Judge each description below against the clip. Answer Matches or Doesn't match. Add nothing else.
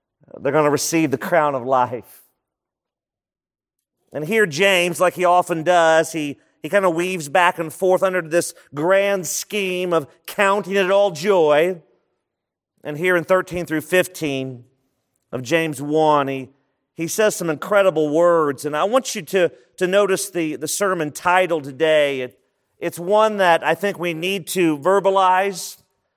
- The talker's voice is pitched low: Doesn't match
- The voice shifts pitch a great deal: Doesn't match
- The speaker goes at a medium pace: Matches